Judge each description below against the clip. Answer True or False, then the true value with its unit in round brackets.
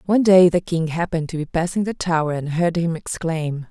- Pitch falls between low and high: True (170 Hz)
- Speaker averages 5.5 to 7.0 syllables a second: True (5.6 syllables/s)